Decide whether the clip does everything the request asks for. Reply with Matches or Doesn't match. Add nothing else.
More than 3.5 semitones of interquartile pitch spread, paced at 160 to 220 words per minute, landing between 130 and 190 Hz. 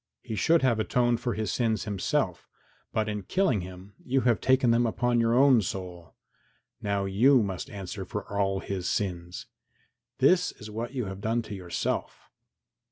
Doesn't match